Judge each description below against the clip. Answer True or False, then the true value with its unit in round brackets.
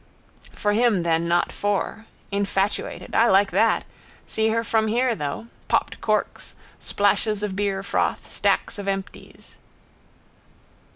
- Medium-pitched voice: False (205 Hz)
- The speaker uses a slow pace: True (120 wpm)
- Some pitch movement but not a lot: False (2.2 semitones)